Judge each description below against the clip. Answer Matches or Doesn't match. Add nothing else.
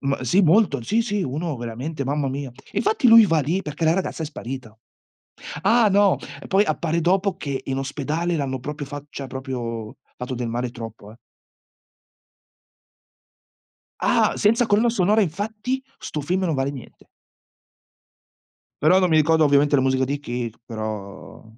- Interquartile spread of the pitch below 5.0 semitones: Doesn't match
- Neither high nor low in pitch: Matches